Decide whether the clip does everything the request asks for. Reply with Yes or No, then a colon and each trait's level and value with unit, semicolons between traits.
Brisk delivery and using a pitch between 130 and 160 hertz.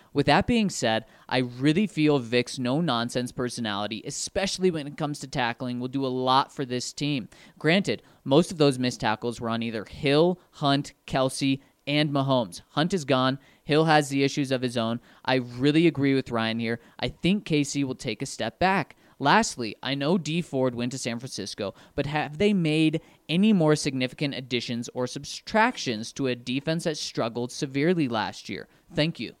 No: average, 185 wpm; medium, 140 Hz